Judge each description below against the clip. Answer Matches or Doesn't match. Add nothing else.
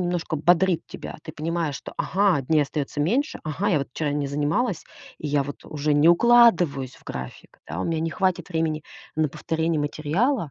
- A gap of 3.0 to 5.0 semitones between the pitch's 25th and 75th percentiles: Matches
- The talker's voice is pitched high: Doesn't match